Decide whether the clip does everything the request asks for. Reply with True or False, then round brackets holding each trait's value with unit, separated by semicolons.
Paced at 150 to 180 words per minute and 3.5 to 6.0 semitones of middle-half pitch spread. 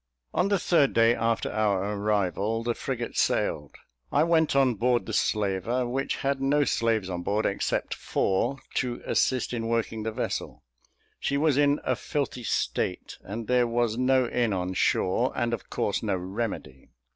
True (170 wpm; 4.0 semitones)